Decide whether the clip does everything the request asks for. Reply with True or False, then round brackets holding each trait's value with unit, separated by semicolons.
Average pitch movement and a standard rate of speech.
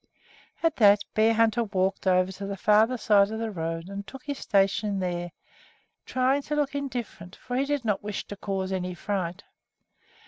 True (4.1 semitones; 175 wpm)